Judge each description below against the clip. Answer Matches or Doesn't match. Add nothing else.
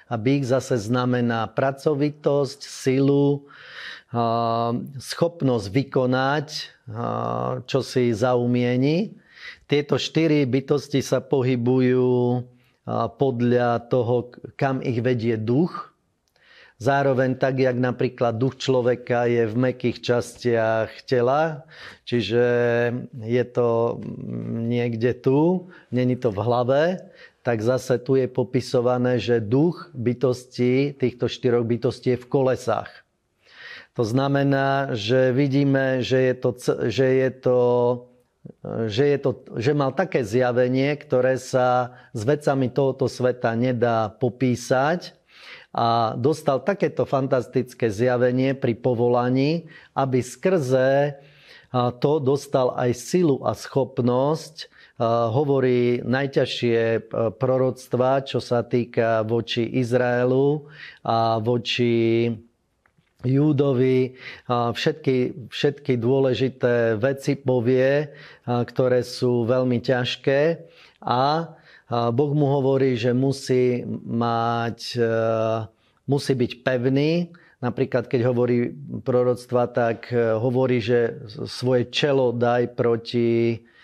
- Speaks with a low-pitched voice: Matches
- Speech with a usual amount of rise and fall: Doesn't match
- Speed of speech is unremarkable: Doesn't match